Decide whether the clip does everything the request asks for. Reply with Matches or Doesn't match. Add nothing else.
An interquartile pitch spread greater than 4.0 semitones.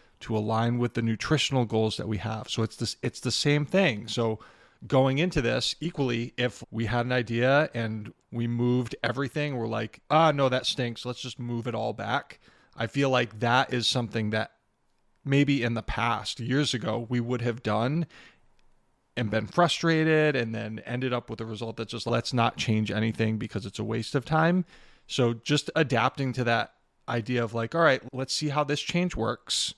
Doesn't match